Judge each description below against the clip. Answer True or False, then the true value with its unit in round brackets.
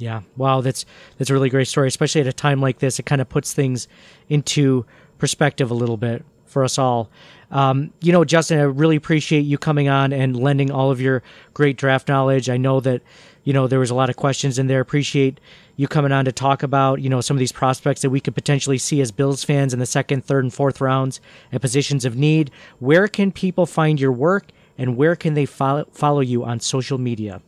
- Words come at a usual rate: False (230 wpm)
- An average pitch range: False (1.8 semitones)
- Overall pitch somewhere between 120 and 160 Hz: True (135 Hz)